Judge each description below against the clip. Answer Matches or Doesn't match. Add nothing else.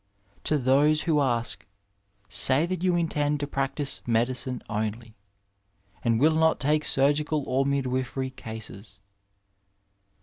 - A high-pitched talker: Doesn't match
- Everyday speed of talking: Doesn't match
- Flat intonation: Doesn't match